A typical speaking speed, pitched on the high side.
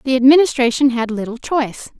Yes: average, 150 wpm; very high, 255 Hz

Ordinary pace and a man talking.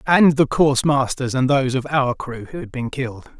No: fast, 230 wpm; male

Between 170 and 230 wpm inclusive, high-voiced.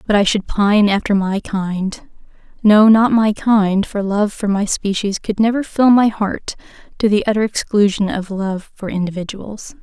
Yes: average, 175 wpm; high, 205 Hz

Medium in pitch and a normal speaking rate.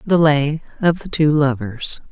Yes: medium, 150 Hz; average, 170 wpm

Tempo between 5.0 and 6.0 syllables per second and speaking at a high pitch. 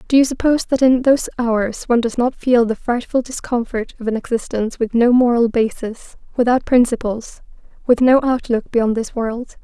Yes: 5.2 syllables/s; high, 240 Hz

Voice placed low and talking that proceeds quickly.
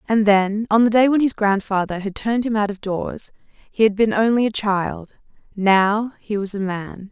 No: high, 210 Hz; fast, 210 wpm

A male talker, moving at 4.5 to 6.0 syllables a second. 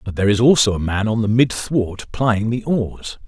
Yes: male; 4.8 syllables/s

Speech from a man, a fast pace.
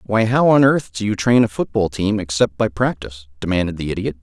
Yes: male; fast, 225 wpm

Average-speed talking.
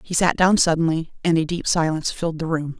No: fast, 235 wpm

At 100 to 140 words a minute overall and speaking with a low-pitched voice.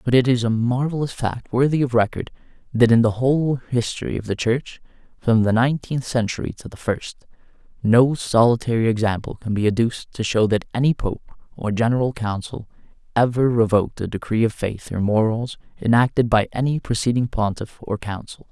No: average, 170 wpm; low, 120 Hz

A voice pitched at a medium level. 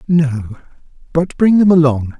Yes: medium, 150 Hz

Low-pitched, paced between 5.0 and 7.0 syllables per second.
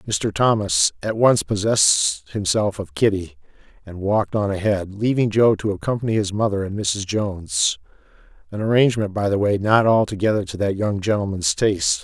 Yes: low, 105 Hz; 5.2 syllables/s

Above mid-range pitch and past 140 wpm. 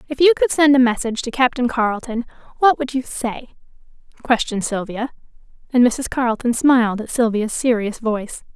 Yes: high, 240 Hz; average, 160 wpm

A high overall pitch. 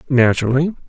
No: low, 135 Hz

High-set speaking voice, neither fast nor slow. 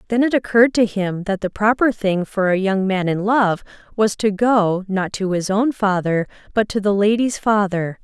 No: high, 205 Hz; fast, 210 wpm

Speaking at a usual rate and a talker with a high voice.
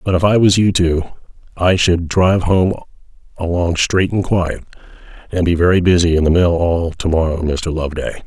No: average, 190 wpm; very low, 85 Hz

